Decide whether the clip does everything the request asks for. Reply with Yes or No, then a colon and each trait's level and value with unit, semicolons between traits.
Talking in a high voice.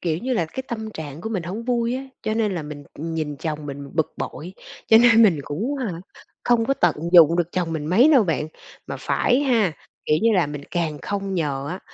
No: medium, 180 Hz